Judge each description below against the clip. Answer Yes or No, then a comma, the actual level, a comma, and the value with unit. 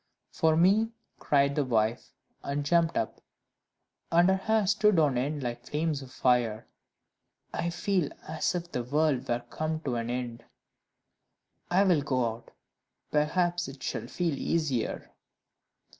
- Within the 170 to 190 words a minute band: No, average, 145 wpm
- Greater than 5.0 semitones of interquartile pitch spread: Yes, wide, 5.6 semitones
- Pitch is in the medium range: Yes, medium, 150 Hz